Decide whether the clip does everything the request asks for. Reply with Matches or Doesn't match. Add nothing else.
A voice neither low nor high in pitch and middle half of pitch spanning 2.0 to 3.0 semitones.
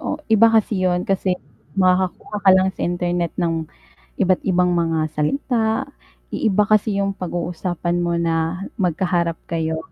Matches